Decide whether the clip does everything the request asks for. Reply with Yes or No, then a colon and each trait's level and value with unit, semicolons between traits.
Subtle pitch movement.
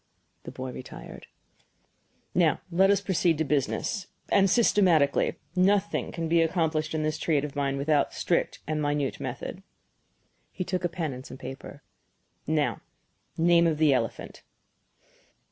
No: average, 3.7 semitones